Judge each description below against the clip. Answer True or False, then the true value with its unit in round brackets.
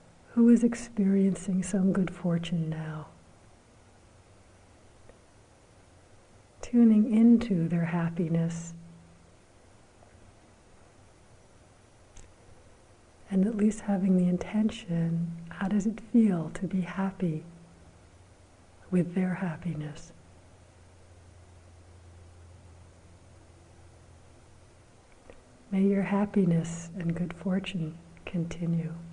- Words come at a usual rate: False (70 wpm)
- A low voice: False (150 Hz)